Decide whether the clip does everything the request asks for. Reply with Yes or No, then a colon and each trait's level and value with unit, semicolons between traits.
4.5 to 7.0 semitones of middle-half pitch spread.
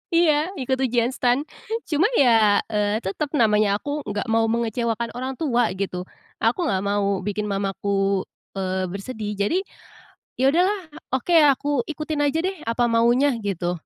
Yes: average, 4.9 semitones